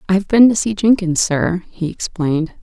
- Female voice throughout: Yes, female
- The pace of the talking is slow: No, fast, 205 wpm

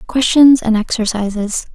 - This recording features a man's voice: No, female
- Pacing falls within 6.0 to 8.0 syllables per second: No, 4.5 syllables/s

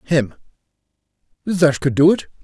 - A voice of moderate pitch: Yes, medium, 150 Hz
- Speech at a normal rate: No, slow, 125 wpm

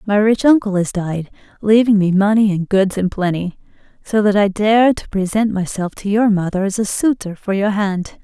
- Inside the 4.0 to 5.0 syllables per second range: Yes, 4.9 syllables/s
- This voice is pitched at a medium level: No, high, 200 Hz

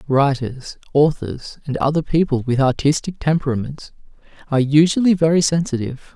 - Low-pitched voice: No, medium, 145 Hz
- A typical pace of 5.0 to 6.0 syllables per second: Yes, 5.4 syllables/s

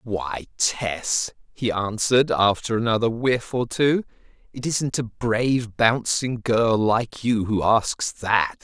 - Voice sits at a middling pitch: No, low, 115 Hz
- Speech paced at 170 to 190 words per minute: No, average, 140 wpm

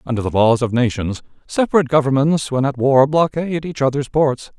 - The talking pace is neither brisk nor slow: Yes, average, 185 wpm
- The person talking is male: Yes, male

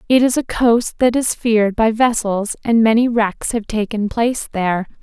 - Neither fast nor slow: Yes, average, 190 wpm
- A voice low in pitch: No, high, 225 Hz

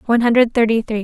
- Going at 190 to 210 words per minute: No, fast, 230 wpm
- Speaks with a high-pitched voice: Yes, high, 230 Hz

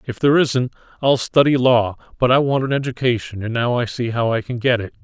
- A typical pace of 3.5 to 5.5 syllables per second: No, 5.7 syllables/s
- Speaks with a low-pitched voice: Yes, low, 125 Hz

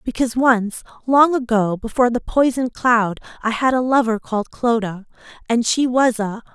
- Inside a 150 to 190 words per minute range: Yes, average, 165 wpm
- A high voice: Yes, high, 235 Hz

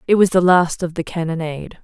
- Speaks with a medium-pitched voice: Yes, medium, 170 Hz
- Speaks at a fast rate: Yes, fast, 230 wpm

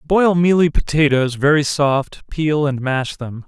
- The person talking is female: No, male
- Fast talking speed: No, average, 155 wpm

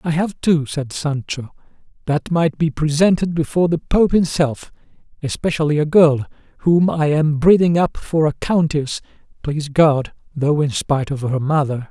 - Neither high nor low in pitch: Yes, medium, 155 Hz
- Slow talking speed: No, average, 160 wpm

